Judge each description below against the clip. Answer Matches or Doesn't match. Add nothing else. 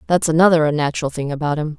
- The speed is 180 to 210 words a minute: Matches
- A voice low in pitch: Doesn't match